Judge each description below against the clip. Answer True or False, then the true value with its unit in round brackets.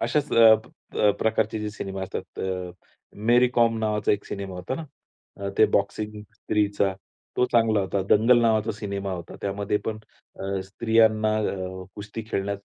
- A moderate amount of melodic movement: False (2.2 semitones)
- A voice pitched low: True (105 Hz)